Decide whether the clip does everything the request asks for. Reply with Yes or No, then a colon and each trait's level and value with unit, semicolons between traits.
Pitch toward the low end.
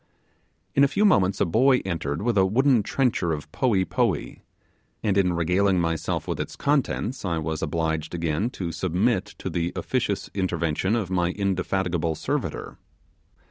Yes: very low, 95 Hz